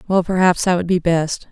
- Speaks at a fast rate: Yes, fast, 240 wpm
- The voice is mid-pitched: Yes, medium, 175 Hz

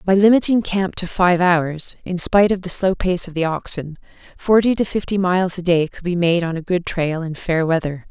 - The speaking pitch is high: No, medium, 180 Hz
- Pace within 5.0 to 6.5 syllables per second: Yes, 5.2 syllables/s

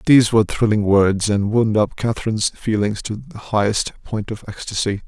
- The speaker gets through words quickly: No, average, 175 wpm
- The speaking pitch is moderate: No, low, 105 Hz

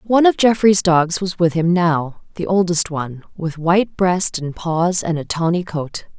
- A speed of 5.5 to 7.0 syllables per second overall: No, 4.5 syllables/s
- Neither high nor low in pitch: Yes, medium, 175 Hz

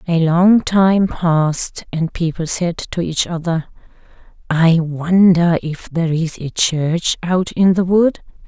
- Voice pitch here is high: No, medium, 170 Hz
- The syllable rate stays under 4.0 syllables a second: Yes, 3.7 syllables/s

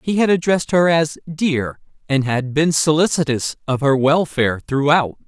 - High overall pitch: No, medium, 150 Hz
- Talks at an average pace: Yes, average, 160 wpm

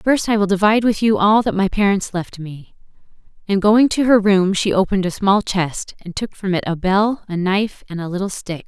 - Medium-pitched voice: No, high, 195 Hz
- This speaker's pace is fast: Yes, fast, 240 wpm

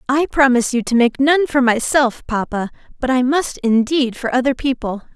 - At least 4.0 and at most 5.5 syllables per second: Yes, 5.1 syllables/s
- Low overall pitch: No, very high, 255 Hz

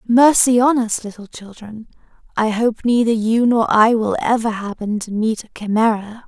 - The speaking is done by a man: No, female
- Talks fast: No, average, 170 wpm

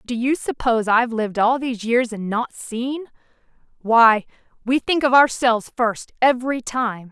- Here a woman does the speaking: Yes, female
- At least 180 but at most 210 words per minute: No, average, 150 wpm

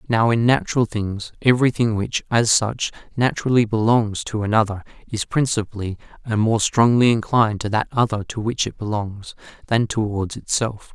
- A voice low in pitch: Yes, low, 110 Hz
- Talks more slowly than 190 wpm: Yes, average, 155 wpm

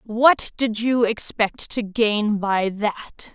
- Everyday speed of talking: Yes, average, 145 wpm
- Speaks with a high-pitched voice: Yes, high, 220 Hz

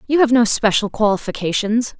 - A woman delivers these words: Yes, female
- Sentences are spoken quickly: No, average, 150 wpm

